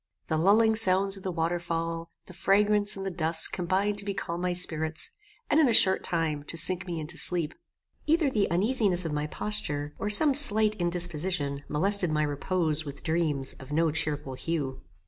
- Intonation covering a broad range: No, average, 4.1 semitones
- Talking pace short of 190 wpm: Yes, average, 180 wpm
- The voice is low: No, medium, 175 Hz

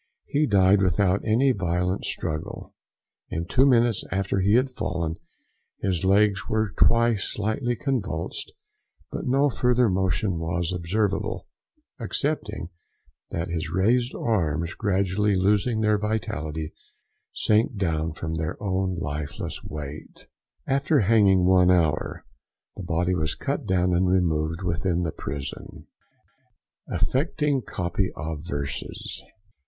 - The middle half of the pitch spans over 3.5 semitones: Yes, average, 4.6 semitones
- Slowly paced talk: Yes, slow, 120 wpm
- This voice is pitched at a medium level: No, very low, 95 Hz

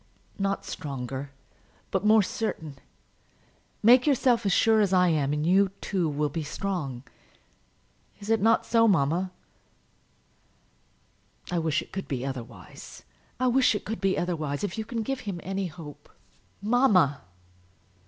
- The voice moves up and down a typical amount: No, wide, 6.6 semitones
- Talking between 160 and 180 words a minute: No, average, 145 wpm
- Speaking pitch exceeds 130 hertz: Yes, medium, 185 Hz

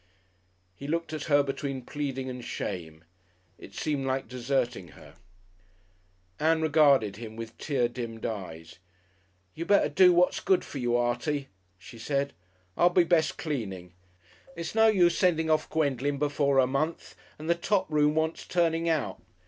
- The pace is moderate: Yes, average, 155 wpm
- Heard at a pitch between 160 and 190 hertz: No, medium, 140 Hz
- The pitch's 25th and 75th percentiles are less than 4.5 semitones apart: No, average, 4.8 semitones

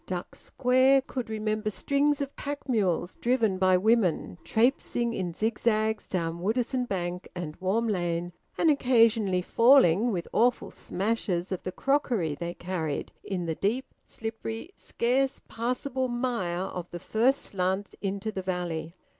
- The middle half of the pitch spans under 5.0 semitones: No, average, 5.3 semitones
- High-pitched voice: Yes, high, 215 Hz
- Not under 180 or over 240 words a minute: No, average, 140 wpm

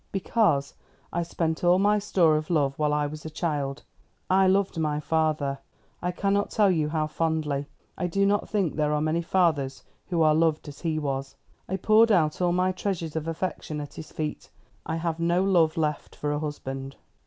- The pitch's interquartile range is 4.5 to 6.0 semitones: No, average, 3.3 semitones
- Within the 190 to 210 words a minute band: Yes, average, 200 wpm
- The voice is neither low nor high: Yes, medium, 160 Hz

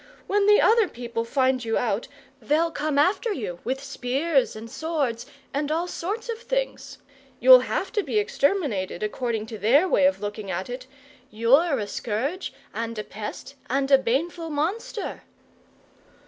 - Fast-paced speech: No, average, 160 wpm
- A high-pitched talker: Yes, very high, 275 Hz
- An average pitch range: No, wide, 6.9 semitones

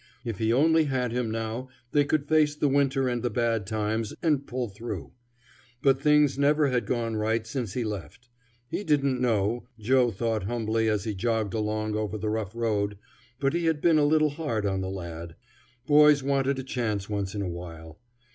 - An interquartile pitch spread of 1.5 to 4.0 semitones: No, average, 4.5 semitones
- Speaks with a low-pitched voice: Yes, low, 115 Hz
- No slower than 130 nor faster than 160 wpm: No, average, 195 wpm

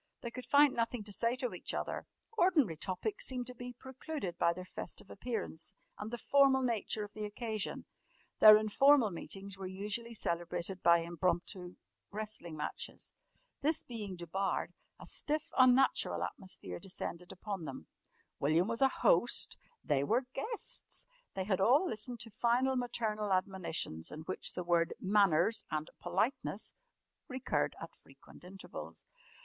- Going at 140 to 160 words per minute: Yes, average, 145 wpm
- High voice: Yes, high, 210 Hz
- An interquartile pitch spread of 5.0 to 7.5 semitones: Yes, wide, 5.5 semitones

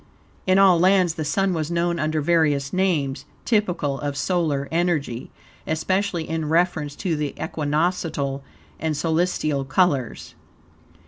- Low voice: No, medium, 160 Hz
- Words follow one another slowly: Yes, slow, 125 wpm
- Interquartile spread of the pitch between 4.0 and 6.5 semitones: No, average, 3.4 semitones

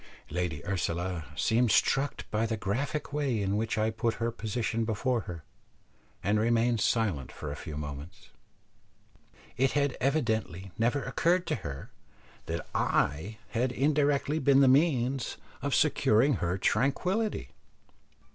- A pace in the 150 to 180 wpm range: No, slow, 135 wpm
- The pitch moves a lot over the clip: Yes, wide, 5.9 semitones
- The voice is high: No, low, 115 Hz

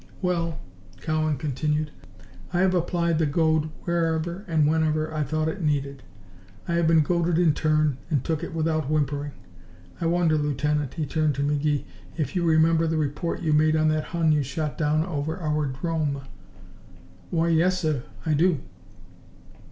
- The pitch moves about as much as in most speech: No, narrow, 1.9 semitones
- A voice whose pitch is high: No, medium, 155 Hz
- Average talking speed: Yes, average, 165 wpm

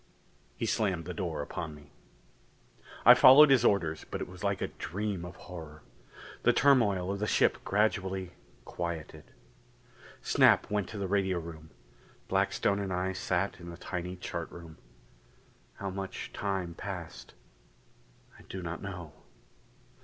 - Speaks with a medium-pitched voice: No, very low, 90 Hz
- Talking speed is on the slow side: No, average, 145 wpm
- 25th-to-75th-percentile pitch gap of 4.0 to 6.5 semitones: No, average, 2.7 semitones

